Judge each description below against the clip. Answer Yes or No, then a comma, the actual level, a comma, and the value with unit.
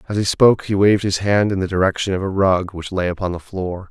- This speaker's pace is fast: Yes, fast, 275 wpm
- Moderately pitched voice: No, very low, 95 Hz